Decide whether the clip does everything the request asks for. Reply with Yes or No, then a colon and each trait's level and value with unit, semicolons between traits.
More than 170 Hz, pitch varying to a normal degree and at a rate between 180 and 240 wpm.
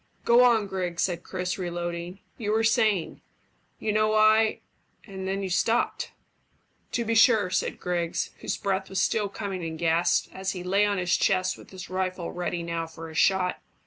Yes: high, 190 Hz; average, 3.0 semitones; average, 185 wpm